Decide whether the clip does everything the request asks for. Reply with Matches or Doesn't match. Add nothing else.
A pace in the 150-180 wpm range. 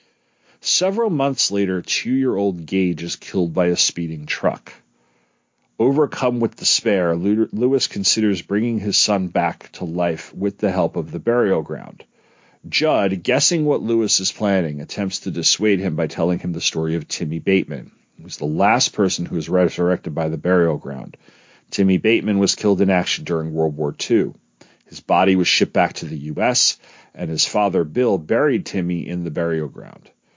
Matches